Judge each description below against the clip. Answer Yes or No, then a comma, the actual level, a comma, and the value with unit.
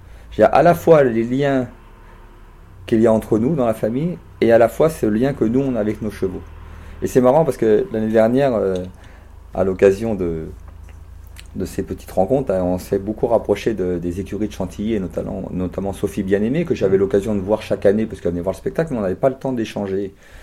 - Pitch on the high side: No, low, 100 Hz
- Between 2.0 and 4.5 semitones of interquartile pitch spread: Yes, average, 3.7 semitones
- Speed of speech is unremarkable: No, fast, 225 wpm